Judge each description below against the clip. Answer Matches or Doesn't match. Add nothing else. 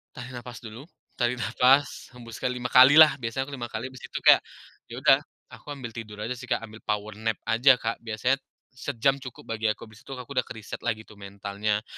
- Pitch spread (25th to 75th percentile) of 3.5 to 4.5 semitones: Doesn't match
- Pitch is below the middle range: Matches